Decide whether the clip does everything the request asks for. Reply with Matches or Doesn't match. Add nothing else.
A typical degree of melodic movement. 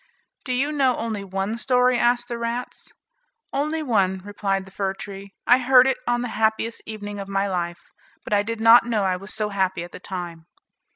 Matches